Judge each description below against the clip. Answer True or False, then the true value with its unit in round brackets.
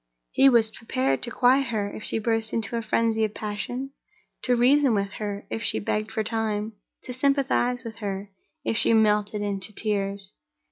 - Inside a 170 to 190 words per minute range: True (180 wpm)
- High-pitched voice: True (220 Hz)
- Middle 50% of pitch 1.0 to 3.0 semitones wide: True (2.5 semitones)